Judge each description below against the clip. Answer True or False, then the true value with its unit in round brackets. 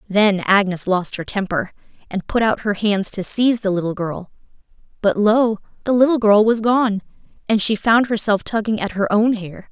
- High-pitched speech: True (210 Hz)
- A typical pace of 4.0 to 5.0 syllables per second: True (4.9 syllables/s)